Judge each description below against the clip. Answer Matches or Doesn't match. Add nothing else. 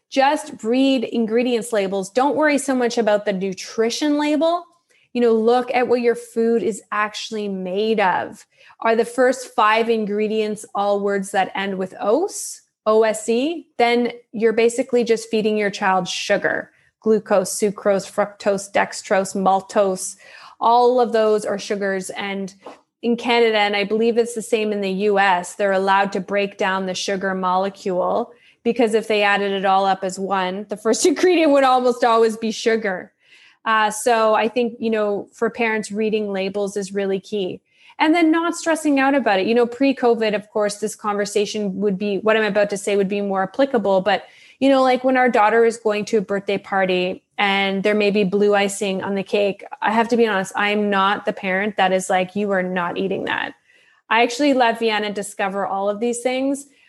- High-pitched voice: Matches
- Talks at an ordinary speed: Matches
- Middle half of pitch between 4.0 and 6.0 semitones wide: Doesn't match